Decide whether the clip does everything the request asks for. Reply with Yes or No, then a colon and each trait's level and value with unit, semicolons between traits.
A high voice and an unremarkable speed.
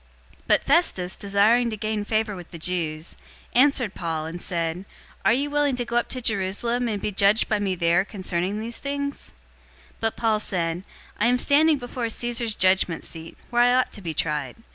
Yes: high, 210 Hz; average, 195 wpm